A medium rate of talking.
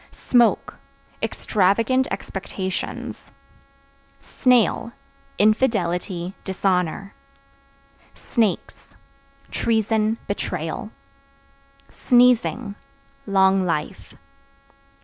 No: slow, 50 wpm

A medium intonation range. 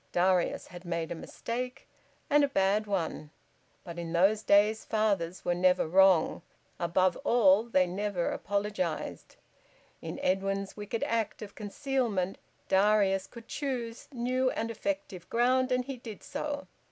Yes: average, 4.2 semitones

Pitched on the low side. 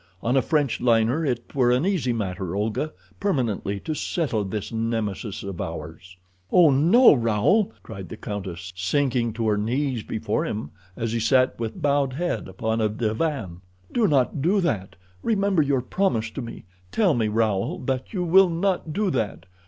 Yes: low, 120 Hz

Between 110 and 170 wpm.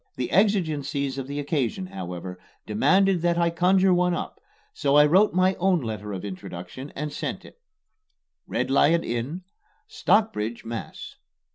Yes: average, 145 wpm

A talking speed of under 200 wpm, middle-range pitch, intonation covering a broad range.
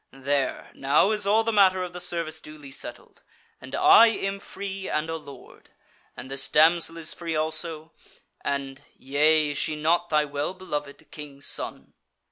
No: average, 165 wpm; medium, 160 Hz; average, 4.0 semitones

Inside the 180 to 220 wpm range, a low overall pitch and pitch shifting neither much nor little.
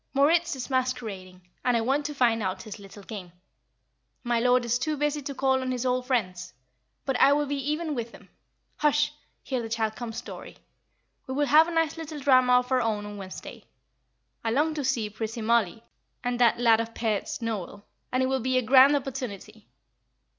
No: average, 195 wpm; very high, 250 Hz; average, 3.7 semitones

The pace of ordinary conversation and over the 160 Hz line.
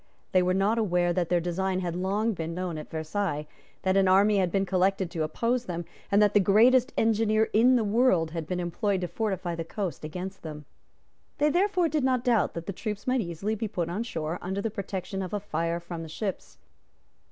No: fast, 215 wpm; high, 190 Hz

